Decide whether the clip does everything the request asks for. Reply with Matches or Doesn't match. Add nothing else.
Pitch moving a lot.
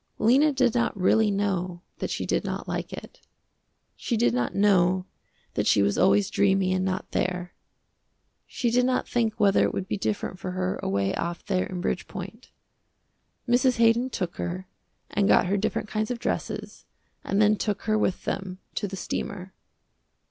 Doesn't match